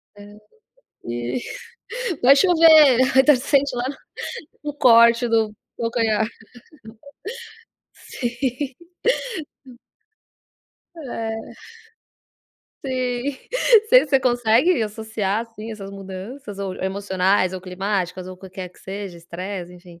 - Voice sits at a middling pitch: No, high, 220 Hz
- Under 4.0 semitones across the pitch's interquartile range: No, average, 5.1 semitones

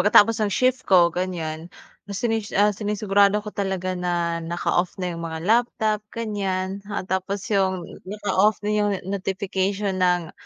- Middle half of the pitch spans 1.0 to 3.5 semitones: Yes, narrow, 2.5 semitones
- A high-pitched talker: Yes, high, 195 Hz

